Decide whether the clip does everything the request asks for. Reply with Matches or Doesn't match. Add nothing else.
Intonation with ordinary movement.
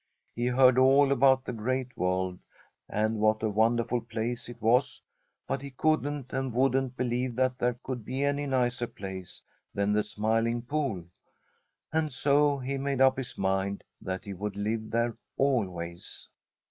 Matches